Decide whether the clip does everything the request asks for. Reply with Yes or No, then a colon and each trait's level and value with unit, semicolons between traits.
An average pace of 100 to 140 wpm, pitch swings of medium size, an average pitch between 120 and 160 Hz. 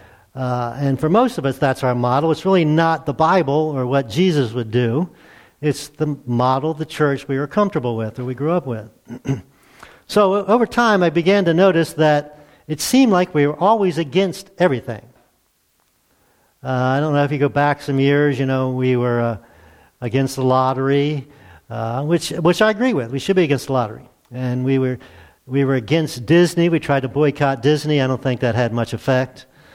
No: average, 200 wpm; average, 4.1 semitones; medium, 140 Hz